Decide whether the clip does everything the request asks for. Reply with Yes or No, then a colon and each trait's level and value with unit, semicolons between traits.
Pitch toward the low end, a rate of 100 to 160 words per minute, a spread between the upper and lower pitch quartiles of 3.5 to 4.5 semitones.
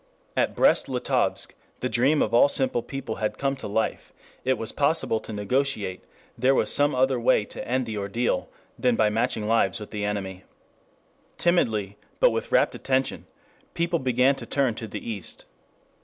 No: low, 120 Hz; average, 170 wpm; average, 3.9 semitones